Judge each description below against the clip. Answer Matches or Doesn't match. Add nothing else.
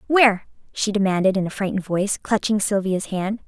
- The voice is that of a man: Doesn't match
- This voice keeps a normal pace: Matches